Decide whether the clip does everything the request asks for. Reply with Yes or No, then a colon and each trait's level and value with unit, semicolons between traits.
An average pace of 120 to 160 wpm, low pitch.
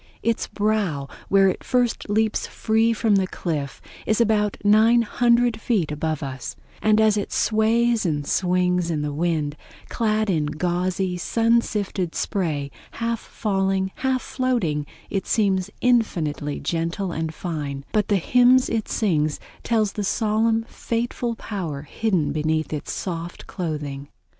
No: average, 140 wpm; high, 195 Hz